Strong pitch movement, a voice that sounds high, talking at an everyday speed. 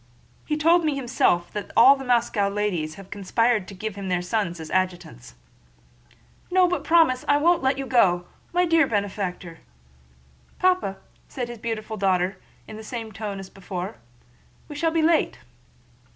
Yes: wide, 6.7 semitones; high, 215 Hz; average, 170 wpm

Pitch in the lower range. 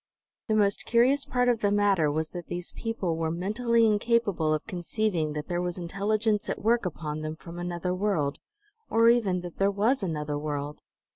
No: medium, 185 Hz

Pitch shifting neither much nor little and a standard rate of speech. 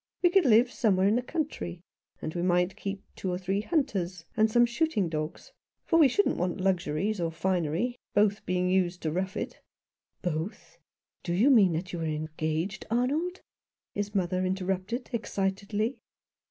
Yes: average, 4.7 semitones; average, 180 wpm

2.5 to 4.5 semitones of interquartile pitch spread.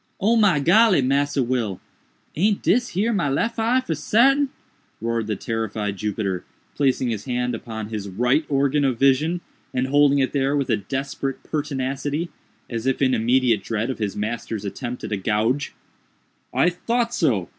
No: average, 5.2 semitones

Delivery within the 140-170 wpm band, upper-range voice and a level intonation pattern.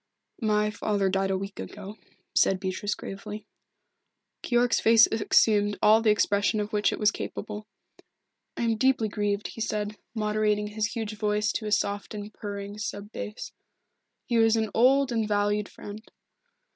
Yes: average, 160 wpm; high, 210 Hz; narrow, 1.1 semitones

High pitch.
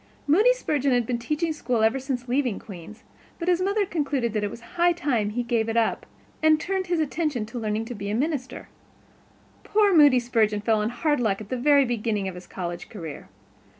Yes: high, 245 Hz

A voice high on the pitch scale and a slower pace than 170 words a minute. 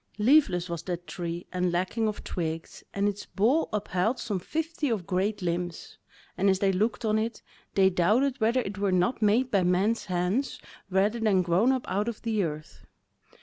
No: high, 200 Hz; average, 190 wpm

